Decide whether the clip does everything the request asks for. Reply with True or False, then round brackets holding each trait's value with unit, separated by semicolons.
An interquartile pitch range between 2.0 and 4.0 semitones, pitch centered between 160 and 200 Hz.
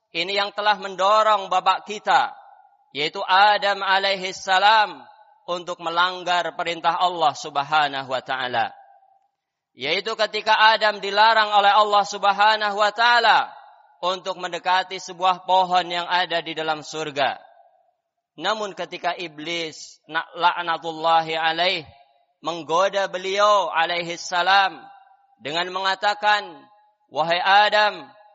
True (3.7 semitones; 190 Hz)